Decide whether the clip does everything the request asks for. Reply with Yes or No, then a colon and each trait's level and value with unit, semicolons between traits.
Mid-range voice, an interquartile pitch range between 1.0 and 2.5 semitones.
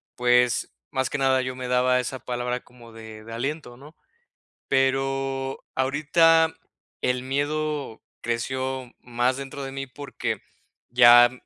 No: low, 130 Hz; narrow, 1.8 semitones